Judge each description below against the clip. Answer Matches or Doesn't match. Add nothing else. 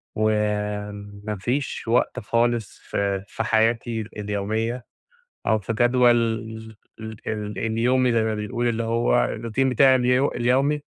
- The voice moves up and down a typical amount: Doesn't match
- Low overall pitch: Matches